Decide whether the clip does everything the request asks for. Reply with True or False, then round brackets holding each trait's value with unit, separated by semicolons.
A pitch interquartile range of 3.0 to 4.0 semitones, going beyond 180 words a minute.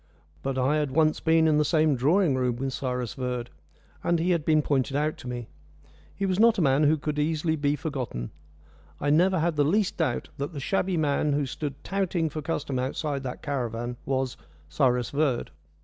True (3.5 semitones; 195 wpm)